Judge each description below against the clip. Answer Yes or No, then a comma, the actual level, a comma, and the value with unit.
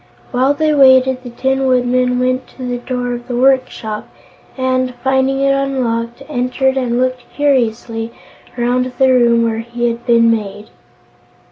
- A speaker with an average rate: Yes, average, 150 wpm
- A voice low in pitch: No, very high, 250 Hz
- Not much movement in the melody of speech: Yes, narrow, 1.7 semitones